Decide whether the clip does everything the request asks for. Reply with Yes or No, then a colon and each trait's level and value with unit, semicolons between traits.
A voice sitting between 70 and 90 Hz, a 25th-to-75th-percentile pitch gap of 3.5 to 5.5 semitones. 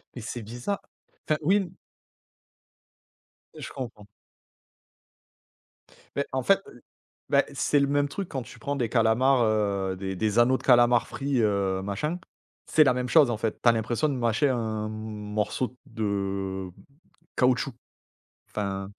No: low, 120 Hz; average, 4.2 semitones